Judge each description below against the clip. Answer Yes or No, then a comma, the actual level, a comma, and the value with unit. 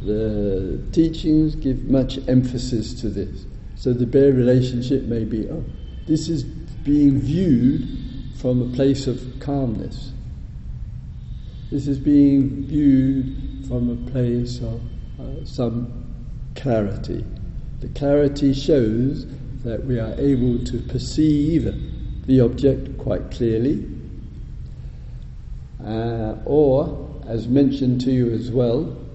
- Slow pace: Yes, slow, 115 wpm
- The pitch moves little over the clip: Yes, narrow, 2.3 semitones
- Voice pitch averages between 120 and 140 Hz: Yes, low, 130 Hz